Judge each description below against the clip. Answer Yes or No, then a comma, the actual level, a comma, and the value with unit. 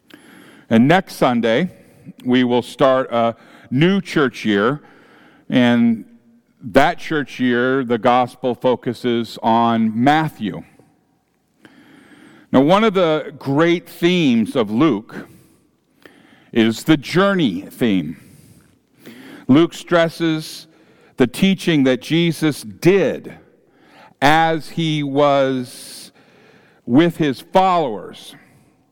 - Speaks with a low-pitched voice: No, medium, 155 Hz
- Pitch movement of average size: No, wide, 6.1 semitones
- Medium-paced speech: No, slow, 90 wpm